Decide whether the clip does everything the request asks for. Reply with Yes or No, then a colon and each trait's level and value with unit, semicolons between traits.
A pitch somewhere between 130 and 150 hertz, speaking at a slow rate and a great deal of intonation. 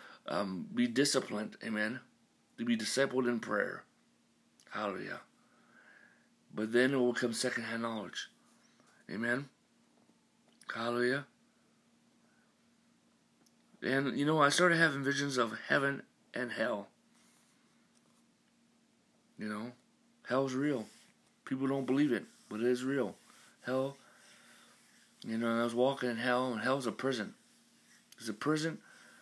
Yes: low, 135 Hz; slow, 120 wpm; wide, 5.8 semitones